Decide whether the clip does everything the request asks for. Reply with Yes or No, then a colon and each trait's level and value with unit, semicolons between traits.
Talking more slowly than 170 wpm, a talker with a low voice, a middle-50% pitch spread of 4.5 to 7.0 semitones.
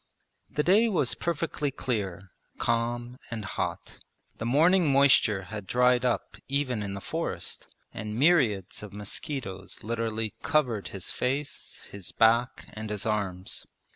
Yes: slow, 135 wpm; low, 115 Hz; average, 4.9 semitones